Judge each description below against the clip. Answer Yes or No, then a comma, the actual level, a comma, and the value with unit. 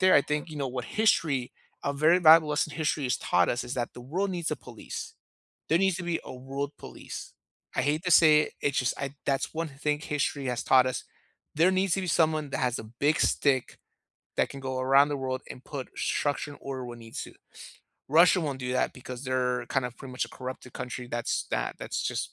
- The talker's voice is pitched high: No, medium, 140 Hz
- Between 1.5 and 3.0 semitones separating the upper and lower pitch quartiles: No, average, 3.5 semitones